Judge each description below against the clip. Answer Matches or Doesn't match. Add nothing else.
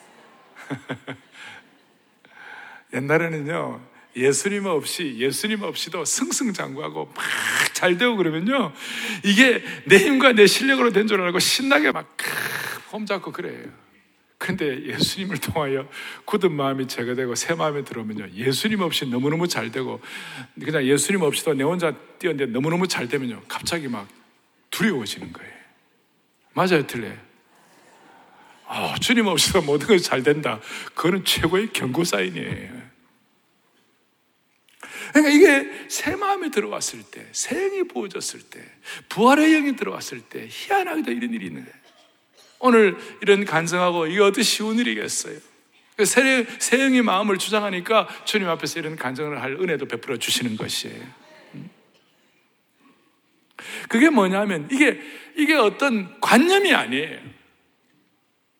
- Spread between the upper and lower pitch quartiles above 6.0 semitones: Matches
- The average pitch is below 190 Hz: Doesn't match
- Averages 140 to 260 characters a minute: Doesn't match